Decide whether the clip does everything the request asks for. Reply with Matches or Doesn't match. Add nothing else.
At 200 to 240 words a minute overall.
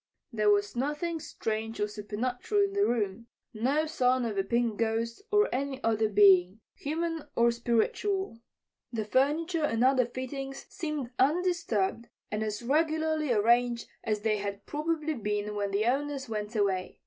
Doesn't match